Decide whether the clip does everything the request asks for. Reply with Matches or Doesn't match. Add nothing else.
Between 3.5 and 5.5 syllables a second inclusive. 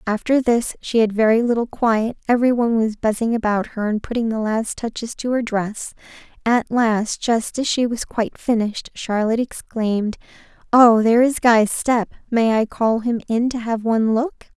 Matches